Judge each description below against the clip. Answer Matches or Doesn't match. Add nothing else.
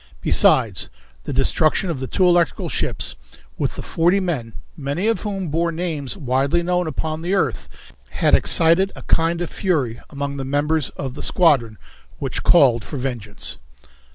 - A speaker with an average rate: Matches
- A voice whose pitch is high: Doesn't match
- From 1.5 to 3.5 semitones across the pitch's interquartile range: Doesn't match